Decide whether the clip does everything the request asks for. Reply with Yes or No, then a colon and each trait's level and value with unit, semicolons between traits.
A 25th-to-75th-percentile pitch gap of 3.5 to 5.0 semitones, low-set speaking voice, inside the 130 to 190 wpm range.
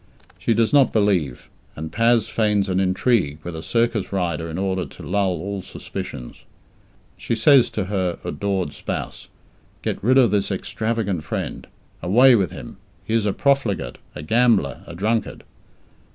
Yes: average, 4.3 semitones; low, 100 Hz; average, 155 wpm